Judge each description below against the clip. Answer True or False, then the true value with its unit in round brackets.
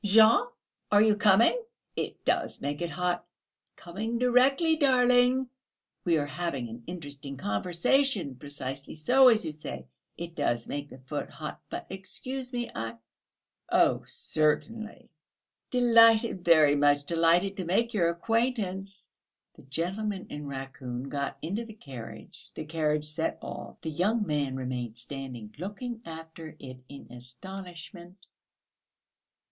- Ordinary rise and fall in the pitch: False (7.5 semitones)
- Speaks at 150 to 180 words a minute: False (135 wpm)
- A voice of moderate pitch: True (170 Hz)